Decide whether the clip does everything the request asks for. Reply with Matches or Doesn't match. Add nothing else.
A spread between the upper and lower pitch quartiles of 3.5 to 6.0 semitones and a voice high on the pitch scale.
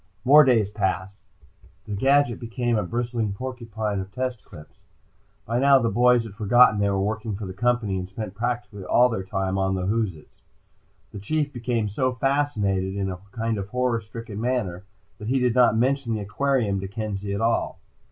Doesn't match